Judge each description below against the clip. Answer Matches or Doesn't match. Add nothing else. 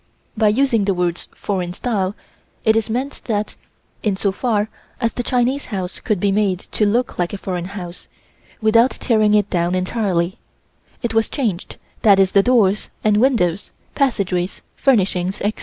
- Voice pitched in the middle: Doesn't match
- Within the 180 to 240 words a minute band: Doesn't match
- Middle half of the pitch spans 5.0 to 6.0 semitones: Doesn't match